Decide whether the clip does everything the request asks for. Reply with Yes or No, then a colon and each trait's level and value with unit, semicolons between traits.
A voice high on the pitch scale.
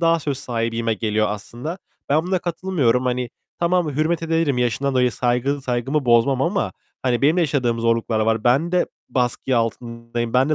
No: low, 125 Hz